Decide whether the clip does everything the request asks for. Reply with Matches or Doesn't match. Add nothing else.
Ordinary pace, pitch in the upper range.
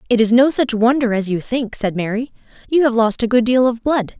Doesn't match